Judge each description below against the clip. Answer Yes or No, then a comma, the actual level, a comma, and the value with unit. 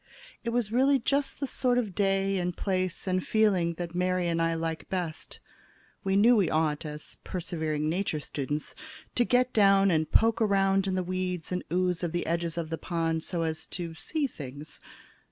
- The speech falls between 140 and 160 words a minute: No, average, 190 wpm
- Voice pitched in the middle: Yes, medium, 180 Hz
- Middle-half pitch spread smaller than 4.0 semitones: Yes, average, 3.3 semitones